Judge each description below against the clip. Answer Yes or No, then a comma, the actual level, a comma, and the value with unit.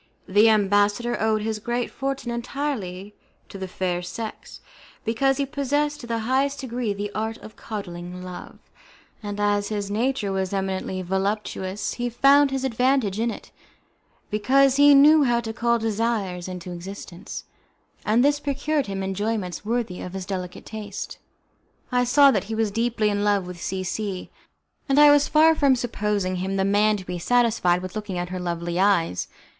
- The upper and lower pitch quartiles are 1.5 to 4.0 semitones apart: No, average, 4.4 semitones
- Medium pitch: No, high, 215 Hz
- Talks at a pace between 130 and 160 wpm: No, average, 170 wpm